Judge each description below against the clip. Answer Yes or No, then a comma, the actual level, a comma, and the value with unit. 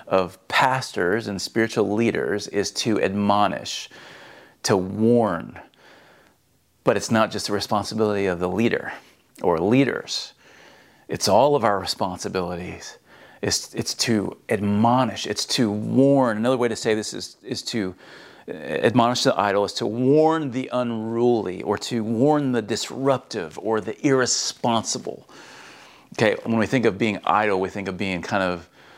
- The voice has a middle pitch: No, low, 110 Hz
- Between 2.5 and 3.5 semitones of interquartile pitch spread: Yes, average, 3.0 semitones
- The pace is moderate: Yes, average, 145 wpm